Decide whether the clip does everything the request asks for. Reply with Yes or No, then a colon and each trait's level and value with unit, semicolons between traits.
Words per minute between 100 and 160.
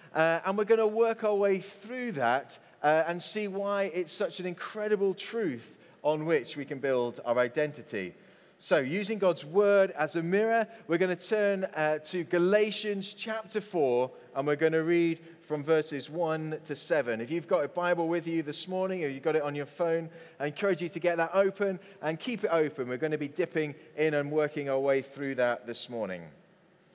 No: fast, 205 wpm